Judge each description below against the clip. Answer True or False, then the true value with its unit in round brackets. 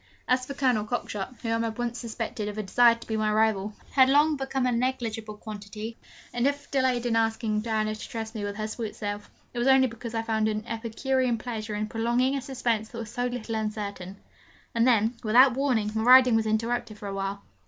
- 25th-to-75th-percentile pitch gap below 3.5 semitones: True (2.5 semitones)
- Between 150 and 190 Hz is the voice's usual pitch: False (225 Hz)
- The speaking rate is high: True (225 wpm)